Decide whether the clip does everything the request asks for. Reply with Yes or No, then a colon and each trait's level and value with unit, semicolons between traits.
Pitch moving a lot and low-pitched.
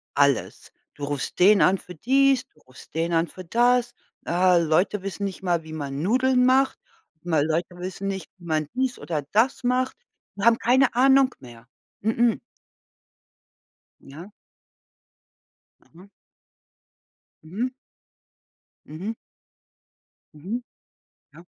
No: wide, 7.3 semitones; high, 190 Hz